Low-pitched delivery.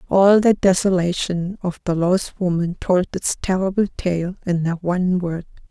No: medium, 180 Hz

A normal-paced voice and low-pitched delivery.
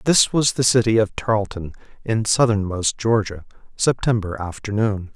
No: slow, 130 wpm; low, 110 Hz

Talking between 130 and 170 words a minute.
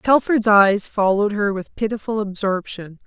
Yes: slow, 135 wpm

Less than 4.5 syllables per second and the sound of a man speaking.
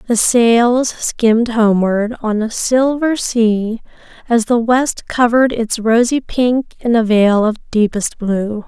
No: 3.6 syllables/s; female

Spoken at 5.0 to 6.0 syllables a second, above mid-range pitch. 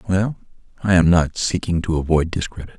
No: 5.6 syllables/s; very low, 90 Hz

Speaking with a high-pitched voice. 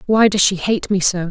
Yes: high, 195 Hz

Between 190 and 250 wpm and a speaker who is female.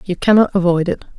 Yes: fast, 205 wpm; female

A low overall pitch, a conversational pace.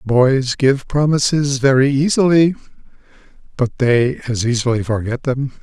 No: low, 130 Hz; slow, 115 wpm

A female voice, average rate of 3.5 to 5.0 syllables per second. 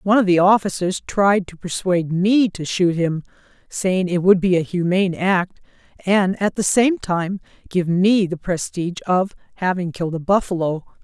Yes: female; 4.9 syllables/s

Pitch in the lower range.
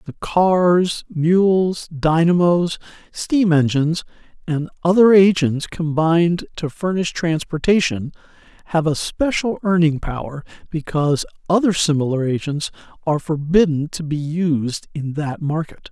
No: medium, 165 Hz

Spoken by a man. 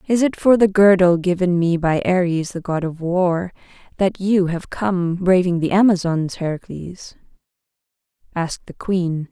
No: female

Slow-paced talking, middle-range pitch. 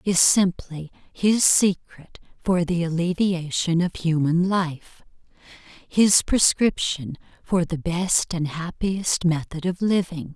Yes: slow, 115 wpm; medium, 175 Hz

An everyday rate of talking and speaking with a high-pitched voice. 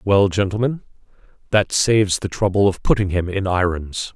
No: average, 160 wpm; very low, 95 Hz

